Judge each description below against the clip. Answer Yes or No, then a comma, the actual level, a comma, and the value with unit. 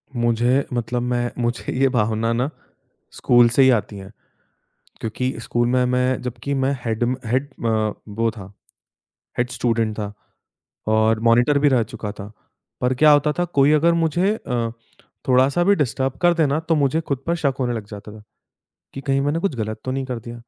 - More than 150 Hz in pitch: No, low, 125 Hz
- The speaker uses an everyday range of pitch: Yes, average, 3.4 semitones